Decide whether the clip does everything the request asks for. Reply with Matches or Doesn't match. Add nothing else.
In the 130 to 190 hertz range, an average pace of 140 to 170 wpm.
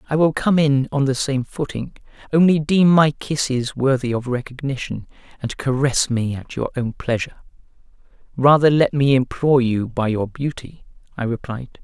Matches